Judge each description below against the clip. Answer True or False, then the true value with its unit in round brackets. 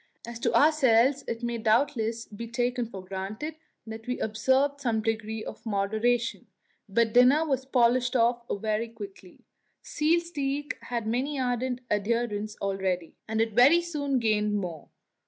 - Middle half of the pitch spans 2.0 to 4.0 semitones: True (3.3 semitones)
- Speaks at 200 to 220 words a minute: False (145 wpm)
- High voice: True (235 Hz)